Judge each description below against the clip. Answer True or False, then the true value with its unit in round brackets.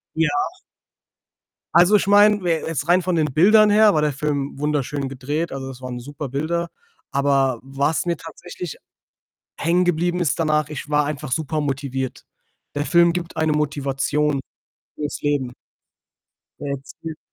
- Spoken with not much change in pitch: False (3.5 semitones)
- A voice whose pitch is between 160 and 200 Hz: False (150 Hz)